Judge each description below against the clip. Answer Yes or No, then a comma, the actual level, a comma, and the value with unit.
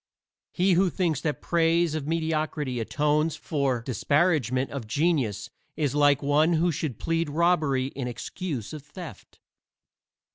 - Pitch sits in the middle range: Yes, medium, 150 Hz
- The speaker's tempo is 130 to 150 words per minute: Yes, slow, 135 wpm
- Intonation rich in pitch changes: No, average, 3.4 semitones